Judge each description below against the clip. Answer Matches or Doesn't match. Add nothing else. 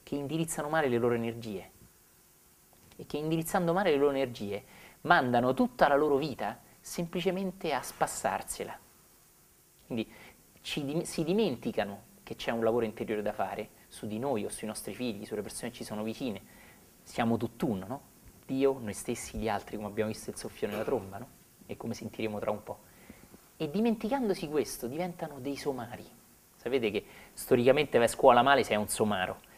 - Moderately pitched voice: Doesn't match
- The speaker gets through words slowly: Doesn't match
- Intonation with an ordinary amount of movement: Doesn't match